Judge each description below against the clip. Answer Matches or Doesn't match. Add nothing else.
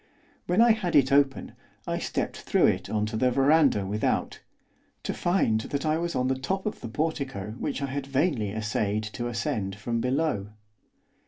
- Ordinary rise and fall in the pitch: Doesn't match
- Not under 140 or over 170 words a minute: Doesn't match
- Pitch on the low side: Matches